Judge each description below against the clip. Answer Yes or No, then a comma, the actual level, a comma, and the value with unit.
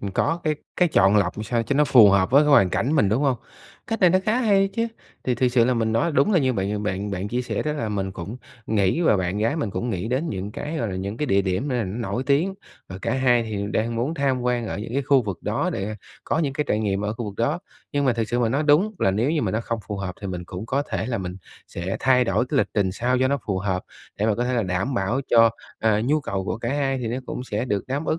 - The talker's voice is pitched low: Yes, low, 115 Hz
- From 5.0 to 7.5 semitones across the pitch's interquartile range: Yes, wide, 5.5 semitones